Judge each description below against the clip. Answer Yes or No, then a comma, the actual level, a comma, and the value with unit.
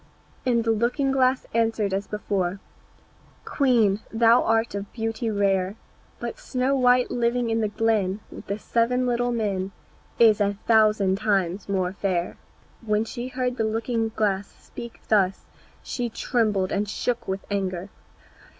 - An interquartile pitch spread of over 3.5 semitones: No, average, 3.1 semitones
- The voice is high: Yes, high, 220 Hz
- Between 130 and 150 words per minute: Yes, average, 145 wpm